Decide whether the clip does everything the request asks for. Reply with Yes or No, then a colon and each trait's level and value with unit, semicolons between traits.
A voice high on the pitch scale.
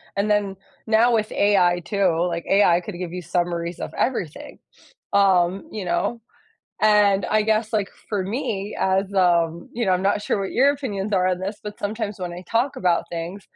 Yes: high, 195 Hz